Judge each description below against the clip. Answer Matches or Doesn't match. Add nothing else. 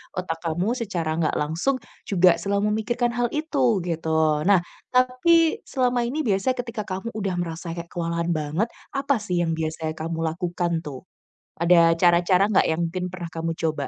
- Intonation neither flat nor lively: Matches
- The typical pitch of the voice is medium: Matches